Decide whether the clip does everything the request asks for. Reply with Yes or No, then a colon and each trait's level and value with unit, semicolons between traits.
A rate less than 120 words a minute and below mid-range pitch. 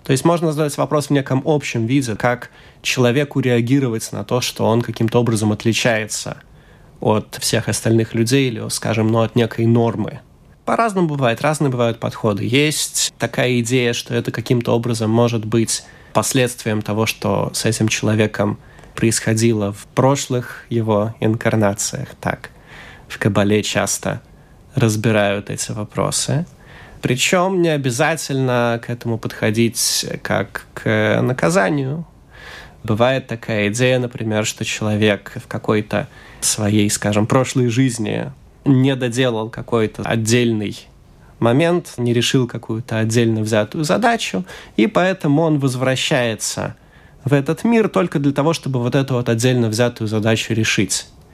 No: average, 130 wpm; low, 120 Hz